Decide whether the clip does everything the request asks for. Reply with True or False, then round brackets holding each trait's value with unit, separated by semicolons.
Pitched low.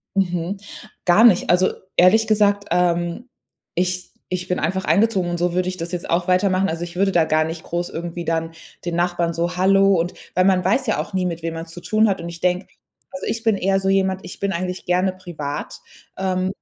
False (180 Hz)